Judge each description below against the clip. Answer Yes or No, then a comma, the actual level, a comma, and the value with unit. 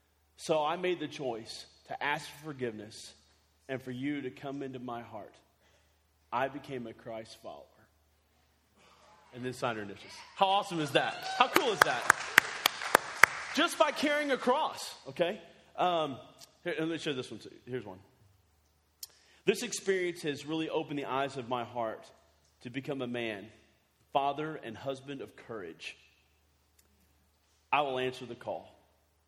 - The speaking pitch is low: Yes, low, 120 Hz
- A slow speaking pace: No, average, 155 wpm